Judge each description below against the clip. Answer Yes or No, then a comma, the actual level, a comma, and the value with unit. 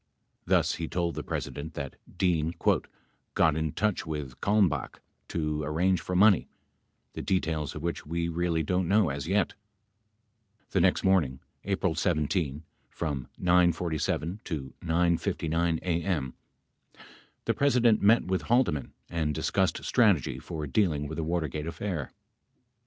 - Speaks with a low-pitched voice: Yes, very low, 85 Hz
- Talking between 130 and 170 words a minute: Yes, average, 140 wpm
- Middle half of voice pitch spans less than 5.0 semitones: Yes, average, 3.3 semitones